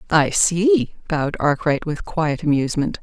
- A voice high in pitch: No, medium, 165 Hz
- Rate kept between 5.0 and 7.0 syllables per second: No, 4.5 syllables/s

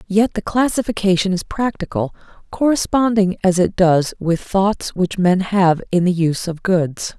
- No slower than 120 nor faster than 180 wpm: Yes, average, 160 wpm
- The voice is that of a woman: Yes, female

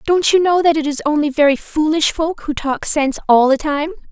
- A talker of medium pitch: No, very high, 300 Hz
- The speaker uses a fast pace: Yes, fast, 235 wpm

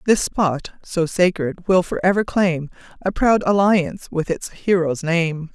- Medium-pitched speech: Yes, medium, 175 Hz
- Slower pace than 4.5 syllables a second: Yes, 4.1 syllables/s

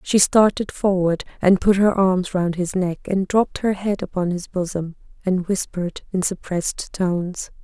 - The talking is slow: No, average, 175 wpm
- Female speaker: Yes, female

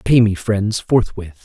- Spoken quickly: No, average, 165 wpm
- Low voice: Yes, low, 105 Hz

